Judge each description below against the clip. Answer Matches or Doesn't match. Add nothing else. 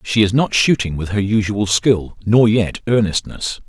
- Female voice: Doesn't match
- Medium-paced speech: Matches